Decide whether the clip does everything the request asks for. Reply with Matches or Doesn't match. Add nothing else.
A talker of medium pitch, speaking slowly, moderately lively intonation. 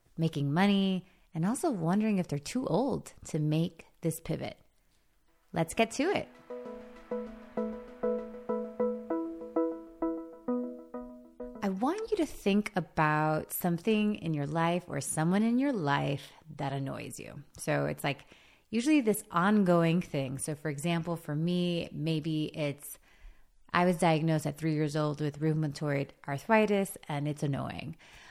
Doesn't match